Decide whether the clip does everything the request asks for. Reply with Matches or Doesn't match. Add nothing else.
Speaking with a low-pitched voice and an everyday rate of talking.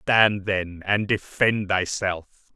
Doesn't match